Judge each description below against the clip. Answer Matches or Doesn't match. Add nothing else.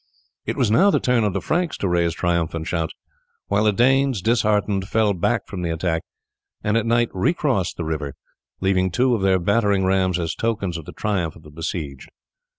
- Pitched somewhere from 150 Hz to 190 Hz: Doesn't match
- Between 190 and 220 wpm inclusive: Matches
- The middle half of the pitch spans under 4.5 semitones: Doesn't match